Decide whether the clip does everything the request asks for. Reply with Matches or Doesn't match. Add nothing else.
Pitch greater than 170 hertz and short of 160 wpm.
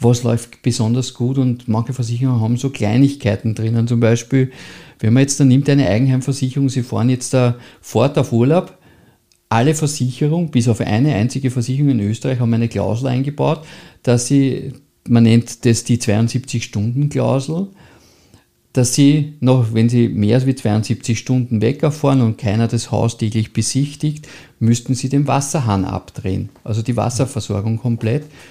Doesn't match